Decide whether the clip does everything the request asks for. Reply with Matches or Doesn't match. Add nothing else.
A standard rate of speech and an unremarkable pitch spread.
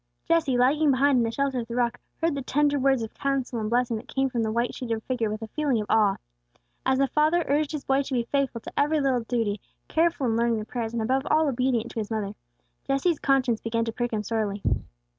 Doesn't match